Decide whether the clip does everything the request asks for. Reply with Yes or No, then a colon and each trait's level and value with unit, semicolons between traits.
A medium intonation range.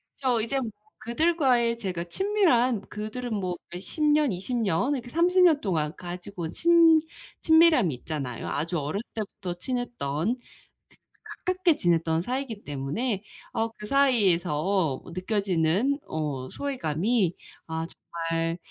No: wide, 7.7 semitones